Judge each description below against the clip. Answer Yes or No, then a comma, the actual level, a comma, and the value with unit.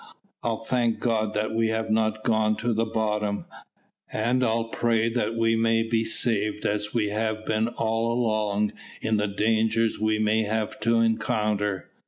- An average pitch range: No, narrow, 1.0 semitones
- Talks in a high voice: No, low, 110 Hz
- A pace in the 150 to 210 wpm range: Yes, average, 165 wpm